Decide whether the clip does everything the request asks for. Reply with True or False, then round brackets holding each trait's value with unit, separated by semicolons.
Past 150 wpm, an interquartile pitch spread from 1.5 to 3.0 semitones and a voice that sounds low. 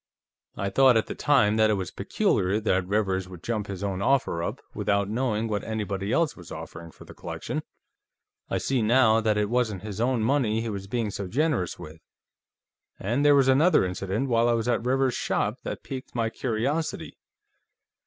False (190 wpm; 4.2 semitones; 110 Hz)